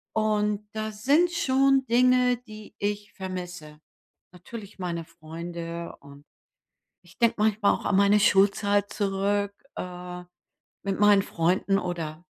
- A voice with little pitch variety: No, average, 3.3 semitones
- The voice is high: Yes, high, 200 Hz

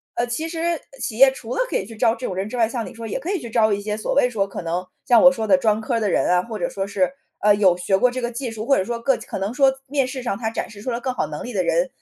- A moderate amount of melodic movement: Yes, average, 3.7 semitones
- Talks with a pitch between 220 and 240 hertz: Yes, high, 230 Hz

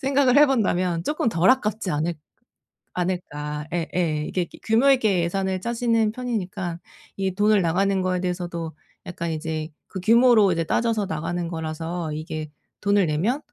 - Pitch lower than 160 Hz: No, medium, 185 Hz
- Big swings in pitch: No, average, 4.8 semitones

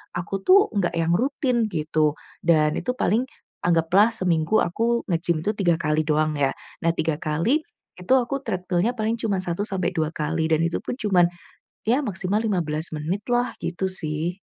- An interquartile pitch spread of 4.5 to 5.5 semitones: Yes, average, 5.2 semitones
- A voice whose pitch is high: No, medium, 175 Hz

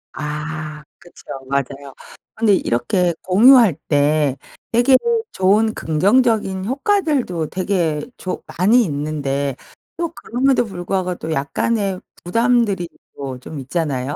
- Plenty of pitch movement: Yes, wide, 7.0 semitones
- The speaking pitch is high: No, medium, 180 Hz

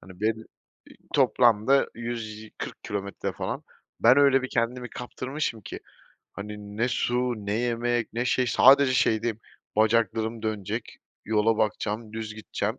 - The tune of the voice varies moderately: No, narrow, 2.2 semitones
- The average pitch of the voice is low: Yes, low, 115 Hz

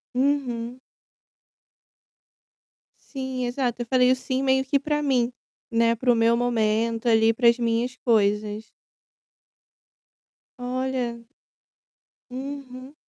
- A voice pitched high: Yes, high, 245 Hz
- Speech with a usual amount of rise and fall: No, narrow, 2.2 semitones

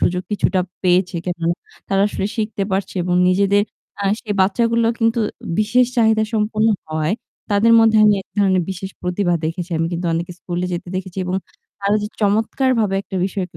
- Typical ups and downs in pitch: Yes, average, 3.1 semitones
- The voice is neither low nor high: No, high, 195 Hz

